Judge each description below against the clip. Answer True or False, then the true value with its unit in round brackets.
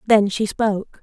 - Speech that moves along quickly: False (175 wpm)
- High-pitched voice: True (210 Hz)